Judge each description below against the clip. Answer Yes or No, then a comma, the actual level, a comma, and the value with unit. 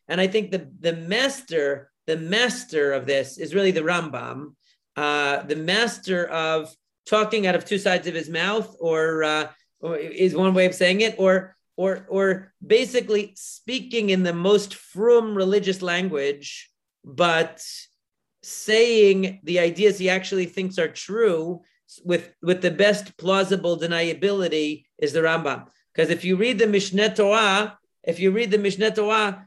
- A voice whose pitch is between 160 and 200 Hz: Yes, high, 190 Hz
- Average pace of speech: Yes, average, 155 wpm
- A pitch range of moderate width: Yes, average, 3.8 semitones